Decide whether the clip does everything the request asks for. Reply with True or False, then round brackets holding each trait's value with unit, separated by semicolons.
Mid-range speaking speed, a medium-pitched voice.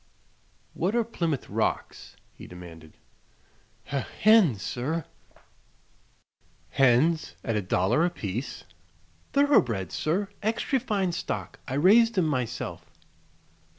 False (100 wpm; 155 Hz)